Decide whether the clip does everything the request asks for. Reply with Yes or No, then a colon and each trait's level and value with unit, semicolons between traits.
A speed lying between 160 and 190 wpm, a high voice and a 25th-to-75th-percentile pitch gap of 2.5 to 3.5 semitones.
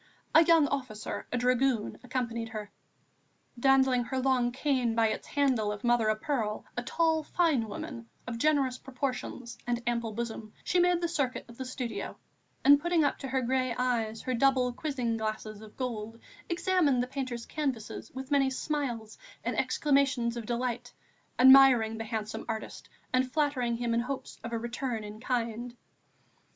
Yes: average, 165 wpm; very high, 250 Hz; average, 2.9 semitones